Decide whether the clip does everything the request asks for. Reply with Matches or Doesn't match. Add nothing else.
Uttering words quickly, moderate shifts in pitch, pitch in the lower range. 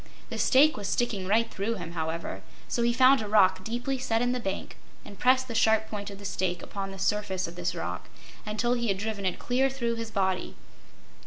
Doesn't match